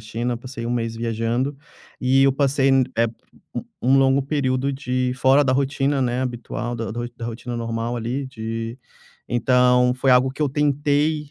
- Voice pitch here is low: Yes, low, 125 Hz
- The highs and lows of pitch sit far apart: No, narrow, 2.5 semitones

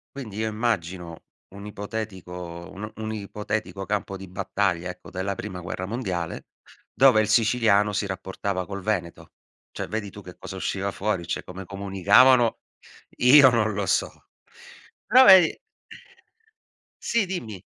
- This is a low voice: Yes, low, 100 Hz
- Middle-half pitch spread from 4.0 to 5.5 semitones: No, average, 2.8 semitones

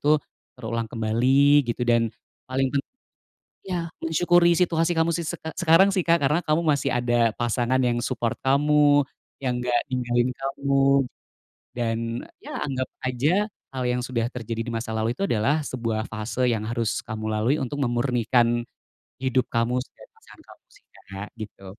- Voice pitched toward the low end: Yes, low, 125 Hz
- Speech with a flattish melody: No, average, 3.5 semitones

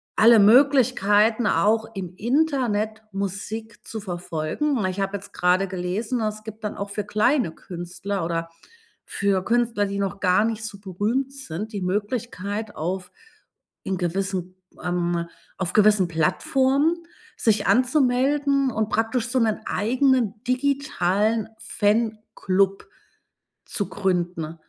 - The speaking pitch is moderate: No, high, 210 Hz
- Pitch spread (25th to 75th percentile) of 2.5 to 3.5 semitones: No, average, 3.9 semitones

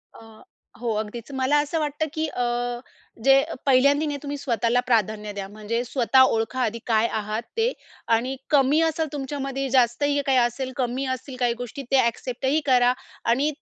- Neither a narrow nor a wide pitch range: Yes, average, 3.4 semitones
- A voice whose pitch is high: Yes, very high, 260 Hz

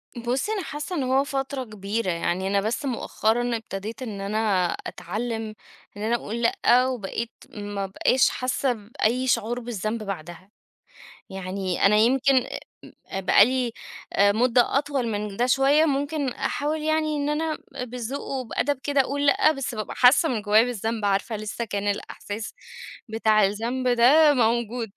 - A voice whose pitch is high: Yes, high, 235 Hz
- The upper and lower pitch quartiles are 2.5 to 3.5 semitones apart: No, average, 4.1 semitones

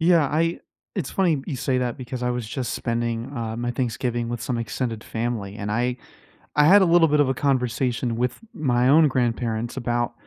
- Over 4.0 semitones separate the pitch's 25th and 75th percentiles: No, average, 2.9 semitones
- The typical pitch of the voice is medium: No, low, 125 Hz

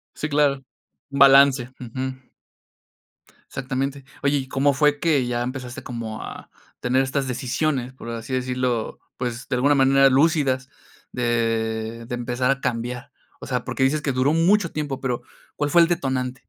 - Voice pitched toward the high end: No, low, 130 Hz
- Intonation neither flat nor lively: No, narrow, 2.2 semitones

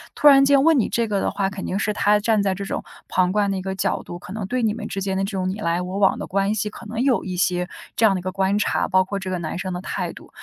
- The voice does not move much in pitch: Yes, narrow, 2.3 semitones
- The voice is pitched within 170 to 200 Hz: Yes, high, 195 Hz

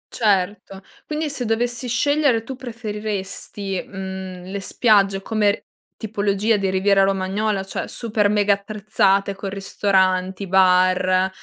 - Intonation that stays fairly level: Yes, narrow, 2.3 semitones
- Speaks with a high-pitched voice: Yes, high, 200 Hz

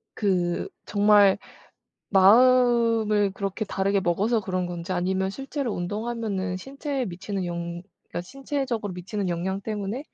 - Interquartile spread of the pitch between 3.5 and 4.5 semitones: Yes, average, 3.8 semitones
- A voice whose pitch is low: No, high, 200 Hz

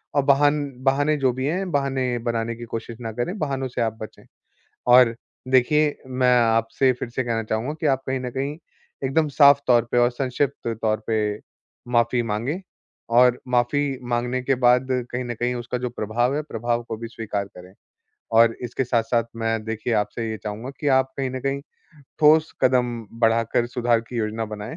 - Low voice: Yes, low, 120 Hz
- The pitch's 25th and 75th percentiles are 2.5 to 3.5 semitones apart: Yes, average, 2.8 semitones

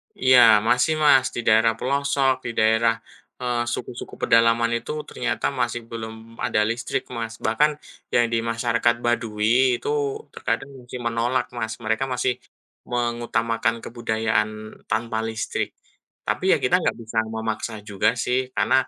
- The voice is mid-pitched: No, low, 115 Hz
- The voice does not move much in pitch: Yes, narrow, 1.7 semitones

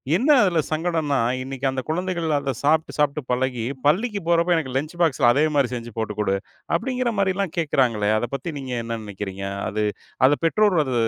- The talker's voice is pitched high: No, medium, 145 Hz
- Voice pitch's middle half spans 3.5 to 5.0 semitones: No, wide, 5.6 semitones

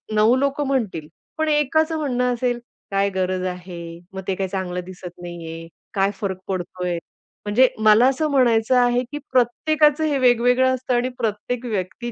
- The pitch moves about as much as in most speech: No, wide, 5.7 semitones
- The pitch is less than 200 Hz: No, high, 235 Hz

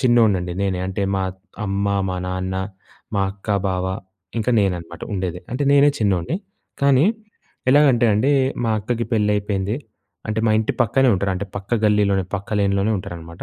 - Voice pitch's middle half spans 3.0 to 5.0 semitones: Yes, average, 3.3 semitones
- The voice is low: Yes, low, 100 Hz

